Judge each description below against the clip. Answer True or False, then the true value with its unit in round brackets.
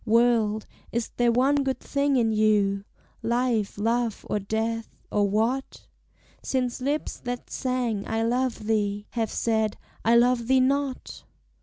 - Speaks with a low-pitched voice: False (230 Hz)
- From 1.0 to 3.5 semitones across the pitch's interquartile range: True (2.7 semitones)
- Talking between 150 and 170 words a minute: False (140 wpm)